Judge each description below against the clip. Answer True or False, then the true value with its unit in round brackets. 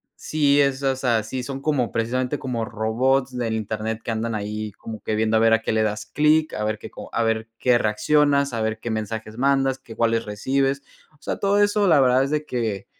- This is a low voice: True (120 Hz)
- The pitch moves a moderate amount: True (3.7 semitones)